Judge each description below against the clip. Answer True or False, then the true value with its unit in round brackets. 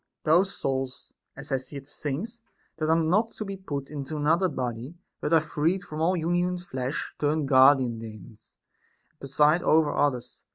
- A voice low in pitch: False (150 Hz)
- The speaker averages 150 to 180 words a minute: True (165 wpm)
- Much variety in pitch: False (4.3 semitones)